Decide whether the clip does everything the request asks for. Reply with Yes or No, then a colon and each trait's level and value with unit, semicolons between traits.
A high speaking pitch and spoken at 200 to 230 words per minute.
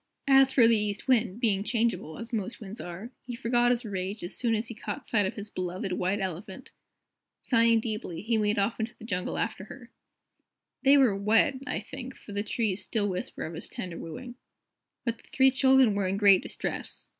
Yes: high, 220 Hz; fast, 205 wpm